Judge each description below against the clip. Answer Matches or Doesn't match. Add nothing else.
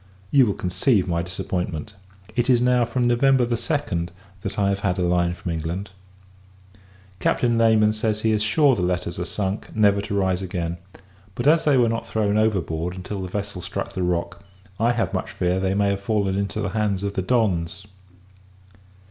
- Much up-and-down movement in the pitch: Doesn't match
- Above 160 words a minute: Matches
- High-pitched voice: Doesn't match